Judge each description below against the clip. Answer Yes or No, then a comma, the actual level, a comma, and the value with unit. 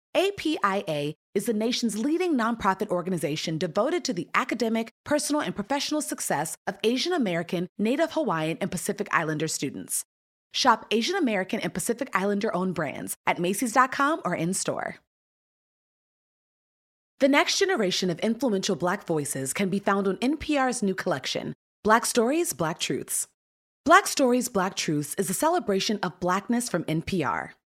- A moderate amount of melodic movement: No, wide, 6.4 semitones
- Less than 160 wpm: Yes, average, 140 wpm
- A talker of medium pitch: No, high, 205 Hz